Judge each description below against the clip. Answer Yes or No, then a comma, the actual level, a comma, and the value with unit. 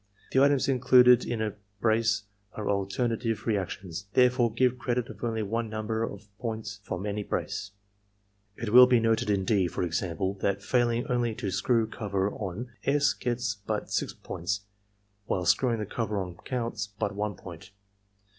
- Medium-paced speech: Yes, average, 165 wpm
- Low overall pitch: Yes, low, 110 Hz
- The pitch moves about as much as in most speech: Yes, average, 3.2 semitones